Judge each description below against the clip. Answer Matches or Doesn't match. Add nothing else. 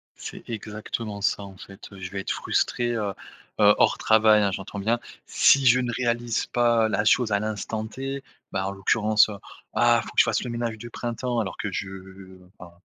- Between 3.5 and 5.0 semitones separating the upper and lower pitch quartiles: Doesn't match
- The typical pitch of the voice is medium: Doesn't match